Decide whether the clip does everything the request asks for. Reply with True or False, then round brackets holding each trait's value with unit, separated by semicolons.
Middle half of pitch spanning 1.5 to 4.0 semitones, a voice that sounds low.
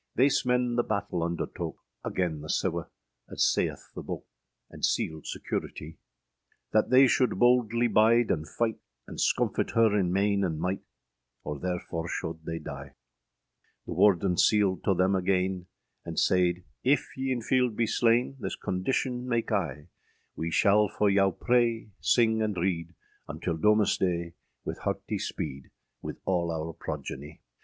False (5.2 semitones; 100 Hz)